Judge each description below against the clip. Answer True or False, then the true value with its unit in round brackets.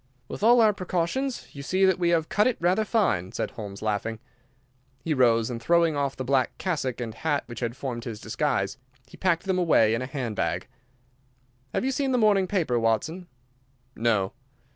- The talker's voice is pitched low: False (145 Hz)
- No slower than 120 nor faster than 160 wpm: False (190 wpm)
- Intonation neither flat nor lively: False (8.1 semitones)